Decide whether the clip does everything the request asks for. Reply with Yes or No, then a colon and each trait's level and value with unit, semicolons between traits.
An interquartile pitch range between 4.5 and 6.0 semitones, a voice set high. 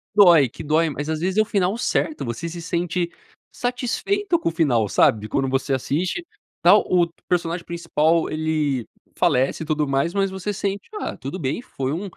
No: average, 4.9 semitones; medium, 165 Hz